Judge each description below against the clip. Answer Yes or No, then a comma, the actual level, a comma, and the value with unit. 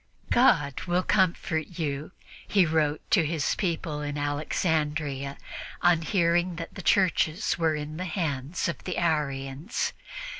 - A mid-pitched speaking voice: Yes, medium, 160 Hz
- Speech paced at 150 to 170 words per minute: No, slow, 135 wpm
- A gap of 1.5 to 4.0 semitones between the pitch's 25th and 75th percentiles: Yes, average, 3.0 semitones